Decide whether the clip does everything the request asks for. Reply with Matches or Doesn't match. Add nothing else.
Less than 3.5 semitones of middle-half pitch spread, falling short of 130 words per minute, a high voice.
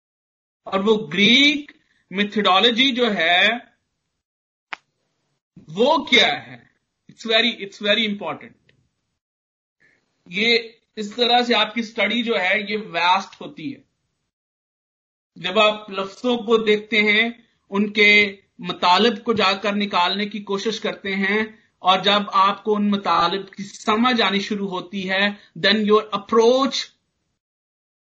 Matches